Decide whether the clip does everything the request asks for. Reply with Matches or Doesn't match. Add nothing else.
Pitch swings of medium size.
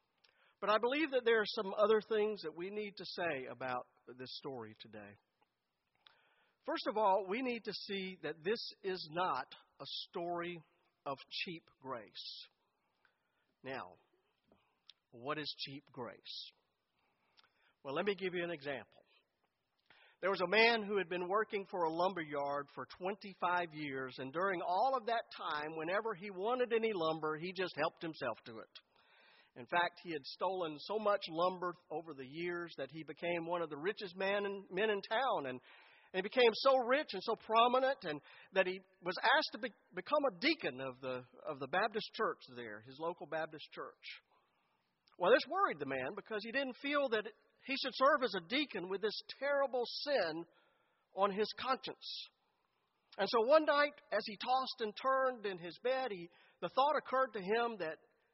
Doesn't match